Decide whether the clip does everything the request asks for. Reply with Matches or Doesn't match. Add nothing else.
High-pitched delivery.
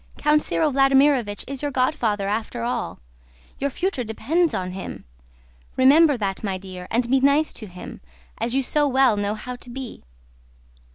Matches